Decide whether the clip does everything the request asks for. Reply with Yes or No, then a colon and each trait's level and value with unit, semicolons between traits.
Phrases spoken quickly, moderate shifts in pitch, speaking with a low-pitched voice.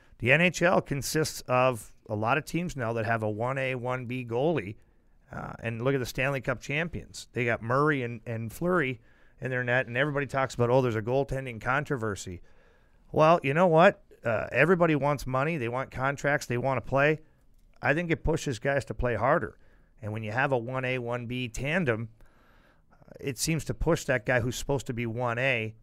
No: average, 195 wpm; average, 3.6 semitones; low, 130 Hz